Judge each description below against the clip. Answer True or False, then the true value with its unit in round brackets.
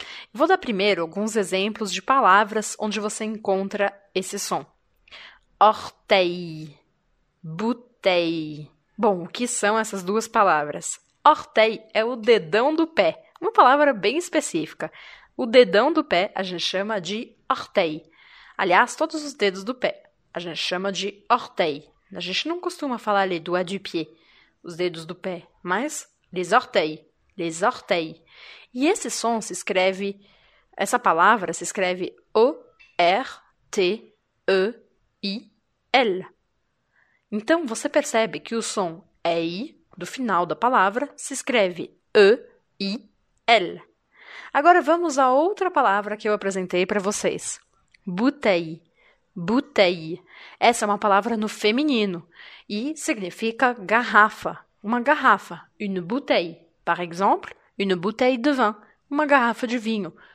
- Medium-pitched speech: False (210 Hz)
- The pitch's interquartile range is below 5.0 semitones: False (5.6 semitones)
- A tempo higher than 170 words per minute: False (125 wpm)